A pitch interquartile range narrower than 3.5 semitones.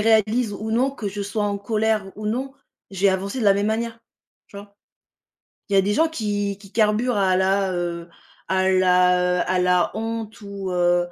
Yes: narrow, 2.6 semitones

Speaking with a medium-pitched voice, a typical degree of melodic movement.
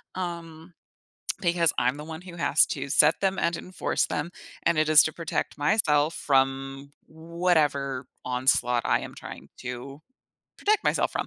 Yes: medium, 155 Hz; average, 3.8 semitones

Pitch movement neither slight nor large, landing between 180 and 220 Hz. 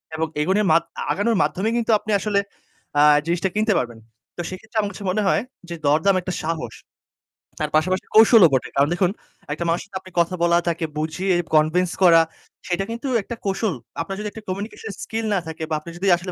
Yes: average, 3.6 semitones; medium, 185 Hz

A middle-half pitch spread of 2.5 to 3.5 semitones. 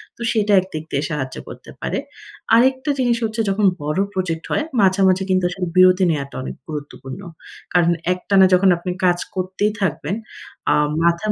Yes: average, 3.2 semitones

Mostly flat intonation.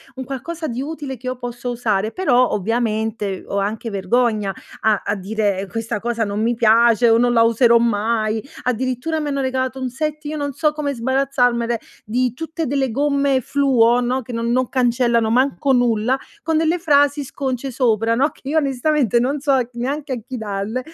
No: average, 3.4 semitones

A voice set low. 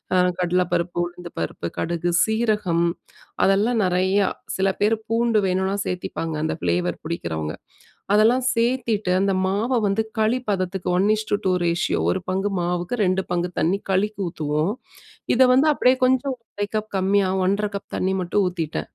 No: high, 190 Hz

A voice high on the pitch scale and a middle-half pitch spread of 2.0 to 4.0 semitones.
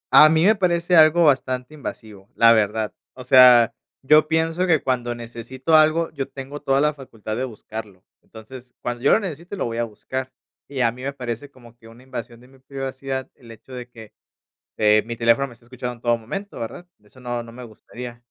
No: low, 125 Hz; average, 3.6 semitones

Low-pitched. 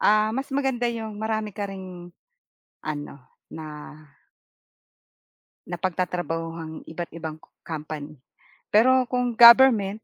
No: high, 195 Hz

